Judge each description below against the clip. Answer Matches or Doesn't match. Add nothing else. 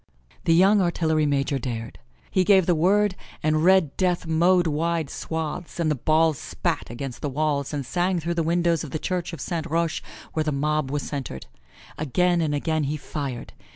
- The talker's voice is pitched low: Doesn't match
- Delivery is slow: Doesn't match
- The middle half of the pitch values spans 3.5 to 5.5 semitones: Doesn't match